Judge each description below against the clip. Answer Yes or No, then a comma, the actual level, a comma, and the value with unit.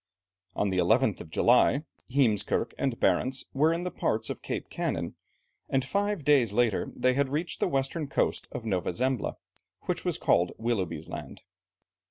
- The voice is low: Yes, low, 125 Hz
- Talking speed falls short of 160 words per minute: No, average, 165 wpm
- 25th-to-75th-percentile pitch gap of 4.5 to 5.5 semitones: Yes, average, 5.2 semitones